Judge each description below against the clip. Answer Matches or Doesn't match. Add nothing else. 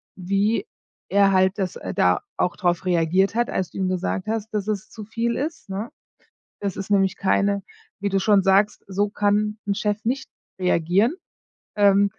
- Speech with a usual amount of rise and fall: Doesn't match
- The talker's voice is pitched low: Doesn't match